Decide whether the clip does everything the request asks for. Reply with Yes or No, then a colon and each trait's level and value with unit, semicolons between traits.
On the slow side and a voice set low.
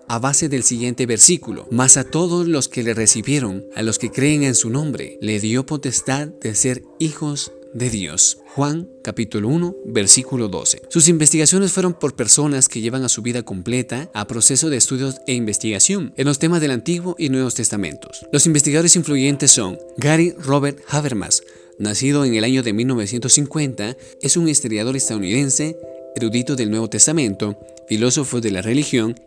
No: average, 170 wpm; low, 130 Hz